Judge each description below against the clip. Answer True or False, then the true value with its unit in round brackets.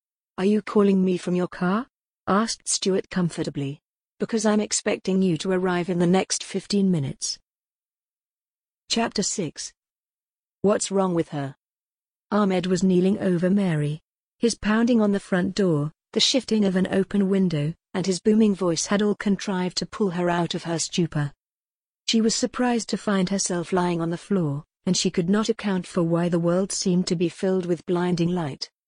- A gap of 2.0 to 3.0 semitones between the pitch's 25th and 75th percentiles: True (2.6 semitones)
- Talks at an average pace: True (175 wpm)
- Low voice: False (185 Hz)